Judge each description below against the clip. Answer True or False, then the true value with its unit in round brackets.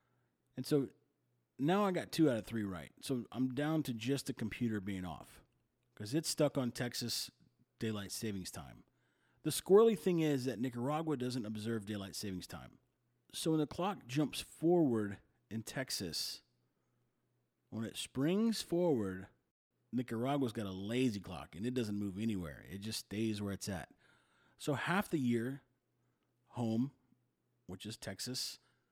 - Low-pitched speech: True (120 Hz)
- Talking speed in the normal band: True (155 wpm)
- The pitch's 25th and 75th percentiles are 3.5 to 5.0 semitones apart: True (4.7 semitones)